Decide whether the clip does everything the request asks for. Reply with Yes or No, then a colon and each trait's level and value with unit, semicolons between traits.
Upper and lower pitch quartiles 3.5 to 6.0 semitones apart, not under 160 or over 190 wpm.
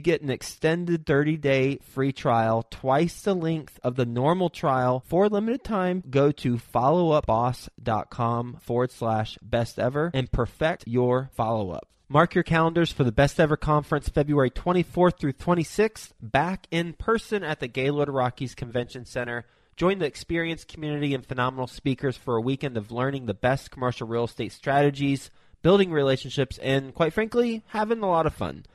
Yes: average, 4.9 semitones; average, 165 wpm